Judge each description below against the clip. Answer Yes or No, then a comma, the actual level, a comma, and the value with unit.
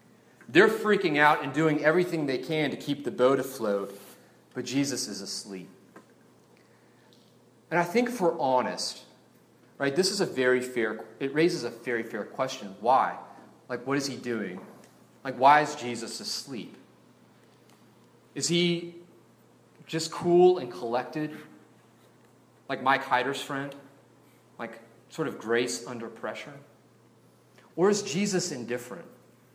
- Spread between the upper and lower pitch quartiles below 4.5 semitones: No, average, 5.0 semitones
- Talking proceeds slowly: Yes, slow, 130 wpm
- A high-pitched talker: No, low, 135 Hz